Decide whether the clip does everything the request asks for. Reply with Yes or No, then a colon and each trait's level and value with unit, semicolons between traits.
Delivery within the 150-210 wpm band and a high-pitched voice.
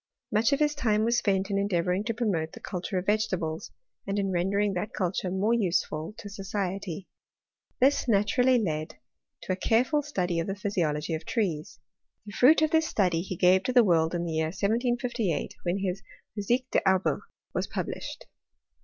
Yes: average, 180 wpm; high, 195 Hz